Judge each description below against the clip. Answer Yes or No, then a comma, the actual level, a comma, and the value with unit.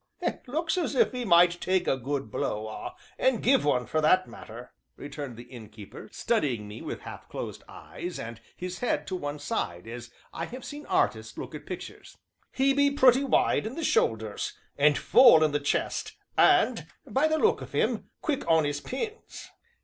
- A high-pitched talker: No, medium, 165 Hz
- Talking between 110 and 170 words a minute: No, average, 185 wpm